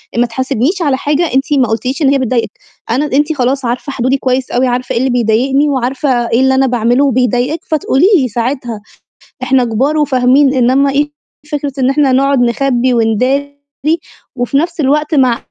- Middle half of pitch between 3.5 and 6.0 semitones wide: No, narrow, 2.4 semitones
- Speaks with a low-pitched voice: No, very high, 260 Hz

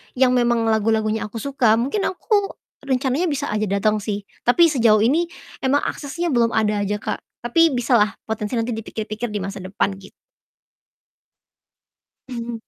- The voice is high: Yes, high, 230 Hz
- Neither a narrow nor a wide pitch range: Yes, average, 3.7 semitones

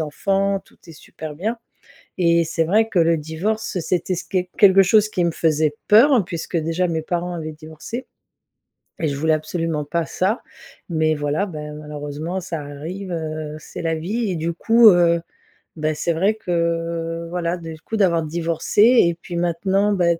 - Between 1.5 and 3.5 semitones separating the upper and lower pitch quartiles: Yes, average, 3.1 semitones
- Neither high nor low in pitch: Yes, medium, 170 Hz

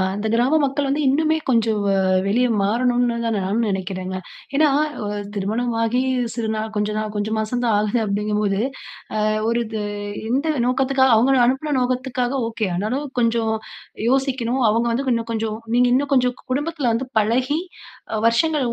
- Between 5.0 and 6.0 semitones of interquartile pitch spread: No, average, 3.4 semitones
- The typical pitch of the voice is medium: No, high, 235 Hz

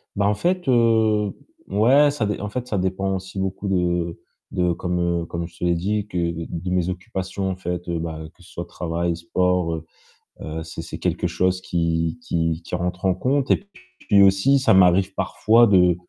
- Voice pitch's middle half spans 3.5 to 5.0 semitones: No, average, 3.1 semitones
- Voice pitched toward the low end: Yes, very low, 90 Hz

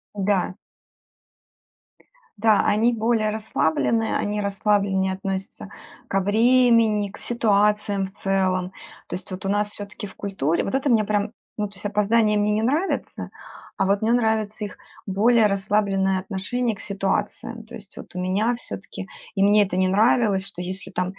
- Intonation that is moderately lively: No, narrow, 2.2 semitones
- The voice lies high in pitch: Yes, high, 205 Hz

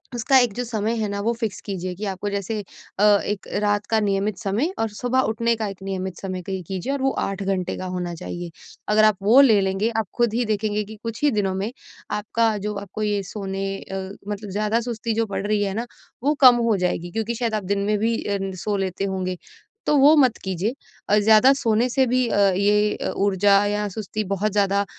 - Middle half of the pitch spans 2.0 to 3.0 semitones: Yes, narrow, 2.6 semitones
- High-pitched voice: Yes, high, 210 Hz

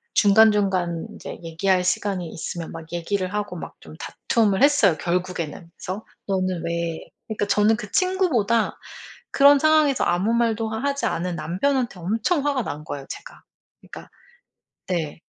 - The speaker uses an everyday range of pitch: Yes, average, 5.0 semitones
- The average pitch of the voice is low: No, high, 200 Hz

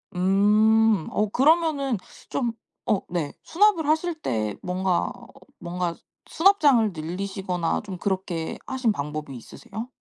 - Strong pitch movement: Yes, wide, 7.0 semitones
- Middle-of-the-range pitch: No, high, 200 Hz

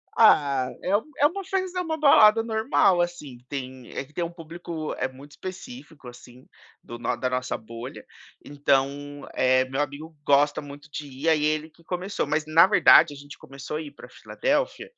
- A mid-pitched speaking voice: Yes, medium, 150 Hz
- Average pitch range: Yes, average, 4.9 semitones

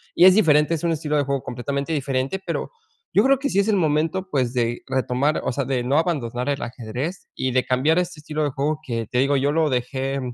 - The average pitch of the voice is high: No, medium, 140 Hz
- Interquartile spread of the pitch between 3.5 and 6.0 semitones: Yes, average, 3.8 semitones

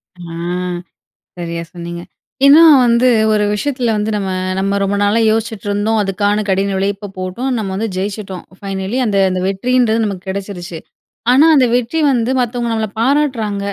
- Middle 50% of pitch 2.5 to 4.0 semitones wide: Yes, average, 3.3 semitones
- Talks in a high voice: Yes, high, 205 Hz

